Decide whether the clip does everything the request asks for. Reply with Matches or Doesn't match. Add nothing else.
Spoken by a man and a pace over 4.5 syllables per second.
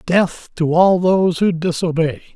Doesn't match